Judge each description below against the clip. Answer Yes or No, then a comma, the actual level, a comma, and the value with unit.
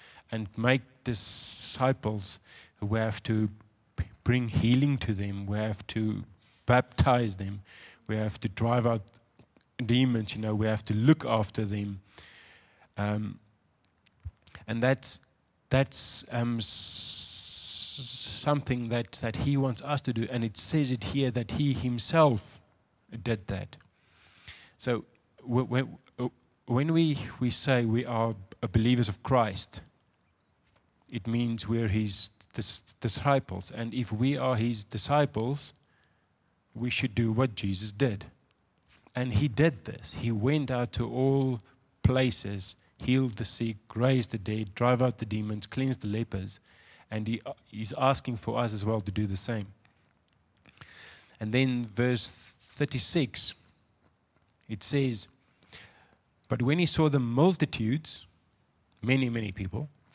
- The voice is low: Yes, low, 115 Hz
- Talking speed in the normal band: No, slow, 130 wpm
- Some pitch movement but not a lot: Yes, average, 3.5 semitones